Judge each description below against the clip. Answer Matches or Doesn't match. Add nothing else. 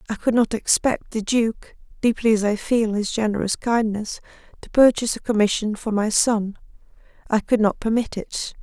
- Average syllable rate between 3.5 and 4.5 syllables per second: Doesn't match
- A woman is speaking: Matches